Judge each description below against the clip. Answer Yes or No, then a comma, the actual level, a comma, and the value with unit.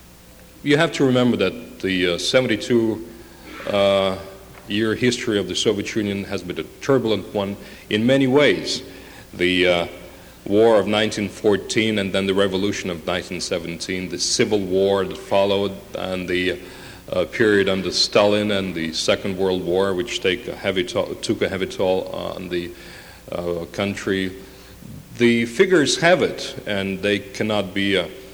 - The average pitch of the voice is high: No, low, 100 Hz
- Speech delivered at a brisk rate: No, average, 150 wpm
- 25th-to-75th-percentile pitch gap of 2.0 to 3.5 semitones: Yes, average, 2.9 semitones